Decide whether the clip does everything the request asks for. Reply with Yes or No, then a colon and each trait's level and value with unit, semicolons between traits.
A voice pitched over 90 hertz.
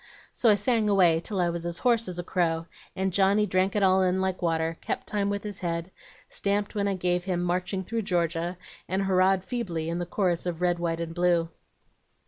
Yes: medium, 185 Hz